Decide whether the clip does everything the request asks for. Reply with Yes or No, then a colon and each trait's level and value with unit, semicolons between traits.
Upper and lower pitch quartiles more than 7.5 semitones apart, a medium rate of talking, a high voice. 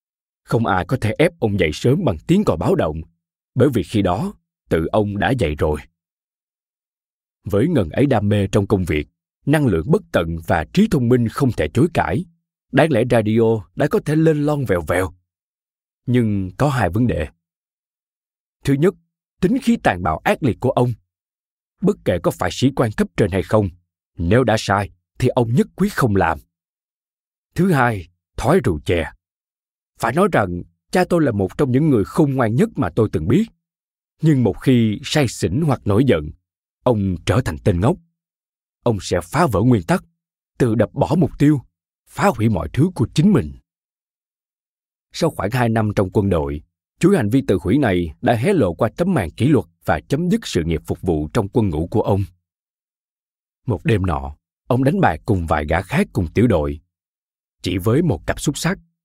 No: wide, 8.7 semitones; average, 195 wpm; low, 115 Hz